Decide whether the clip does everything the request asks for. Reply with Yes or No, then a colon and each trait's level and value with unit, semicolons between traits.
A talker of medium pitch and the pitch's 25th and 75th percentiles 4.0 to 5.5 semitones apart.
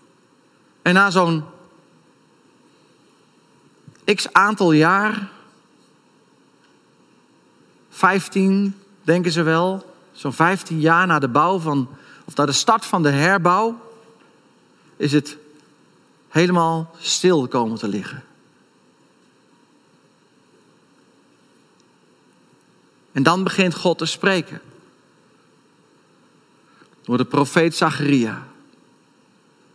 Yes: medium, 170 Hz; average, 4.4 semitones